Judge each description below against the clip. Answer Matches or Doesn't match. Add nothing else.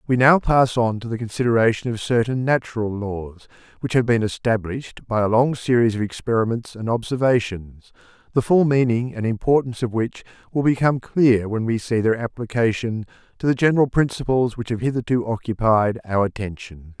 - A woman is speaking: Doesn't match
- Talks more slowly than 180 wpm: Matches